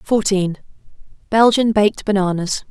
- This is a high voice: Yes, high, 205 Hz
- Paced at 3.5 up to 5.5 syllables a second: Yes, 4.7 syllables/s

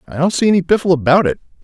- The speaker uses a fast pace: Yes, fast, 255 wpm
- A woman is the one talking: No, male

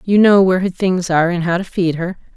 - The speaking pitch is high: No, medium, 180 Hz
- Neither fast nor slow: No, fast, 280 wpm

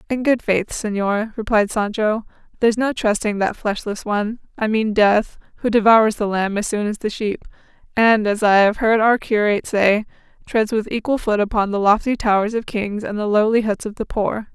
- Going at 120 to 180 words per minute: No, average, 200 wpm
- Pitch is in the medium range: No, high, 215 Hz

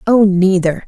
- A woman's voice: Yes, female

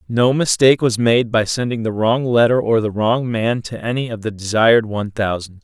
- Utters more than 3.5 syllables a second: Yes, 5.3 syllables/s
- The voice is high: No, low, 115 Hz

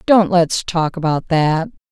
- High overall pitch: No, medium, 170 Hz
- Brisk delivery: No, average, 155 wpm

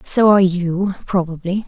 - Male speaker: No, female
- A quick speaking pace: No, average, 145 wpm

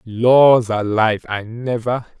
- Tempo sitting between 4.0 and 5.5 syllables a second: No, 3.6 syllables/s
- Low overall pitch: Yes, low, 115 Hz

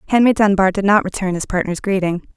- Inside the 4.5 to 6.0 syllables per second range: No, 6.3 syllables/s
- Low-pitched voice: No, high, 195 Hz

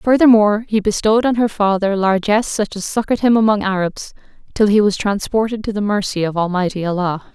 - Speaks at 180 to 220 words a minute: Yes, average, 190 wpm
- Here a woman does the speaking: Yes, female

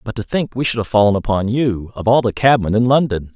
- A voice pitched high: No, low, 115 Hz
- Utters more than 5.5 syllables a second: Yes, 5.9 syllables/s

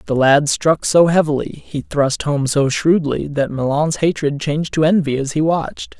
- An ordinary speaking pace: Yes, average, 190 wpm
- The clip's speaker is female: No, male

